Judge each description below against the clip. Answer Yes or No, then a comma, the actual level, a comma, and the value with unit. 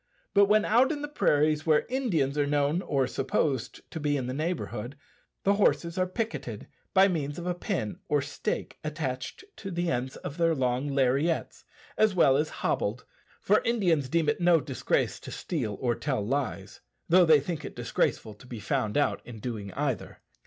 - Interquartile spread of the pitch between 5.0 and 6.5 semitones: Yes, average, 5.3 semitones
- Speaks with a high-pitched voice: No, medium, 150 Hz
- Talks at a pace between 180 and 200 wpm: Yes, average, 185 wpm